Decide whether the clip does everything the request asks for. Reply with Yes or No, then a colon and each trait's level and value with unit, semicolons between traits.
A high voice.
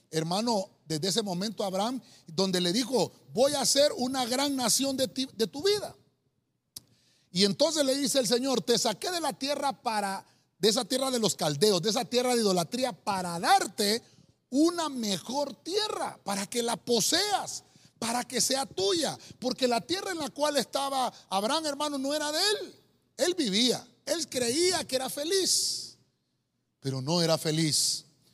Yes: high, 245 Hz